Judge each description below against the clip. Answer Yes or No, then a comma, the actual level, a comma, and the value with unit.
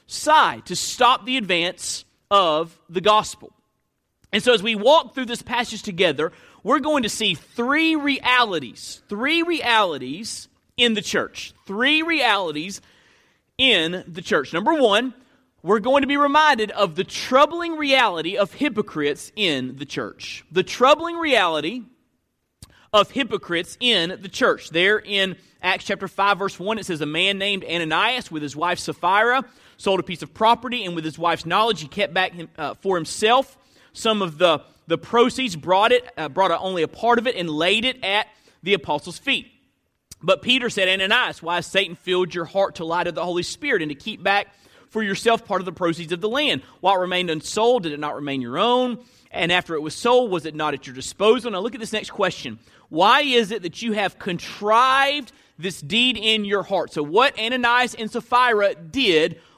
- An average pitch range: No, wide, 5.8 semitones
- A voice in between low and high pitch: No, high, 205 Hz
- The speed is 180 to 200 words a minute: Yes, average, 185 wpm